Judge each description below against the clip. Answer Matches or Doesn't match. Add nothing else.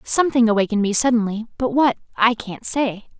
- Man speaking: Doesn't match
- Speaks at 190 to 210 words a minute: Doesn't match